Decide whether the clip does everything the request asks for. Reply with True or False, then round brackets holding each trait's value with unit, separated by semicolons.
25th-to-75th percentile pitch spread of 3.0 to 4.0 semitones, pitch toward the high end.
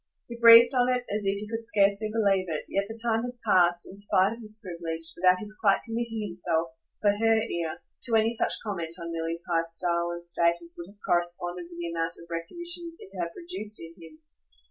False (4.8 semitones; 195 Hz)